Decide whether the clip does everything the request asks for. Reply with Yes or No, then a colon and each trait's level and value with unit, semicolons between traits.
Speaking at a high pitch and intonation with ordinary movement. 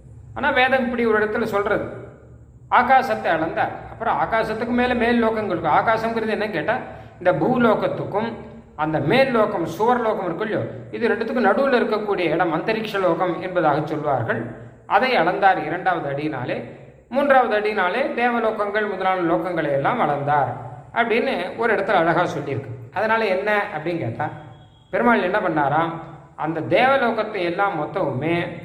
No: high, 195 Hz; wide, 5.9 semitones